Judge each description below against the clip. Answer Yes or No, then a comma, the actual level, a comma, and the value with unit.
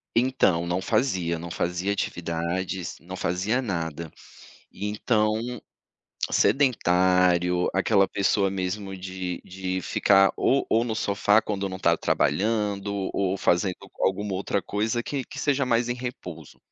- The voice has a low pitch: Yes, very low, 95 Hz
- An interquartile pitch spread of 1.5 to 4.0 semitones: Yes, average, 3.1 semitones